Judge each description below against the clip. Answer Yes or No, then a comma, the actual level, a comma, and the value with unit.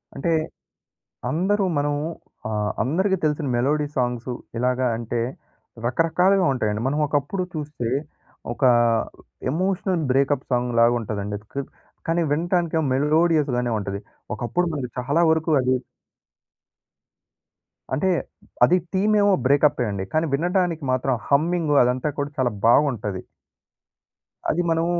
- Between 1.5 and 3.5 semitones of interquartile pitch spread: No, average, 5.2 semitones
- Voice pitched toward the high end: No, medium, 145 Hz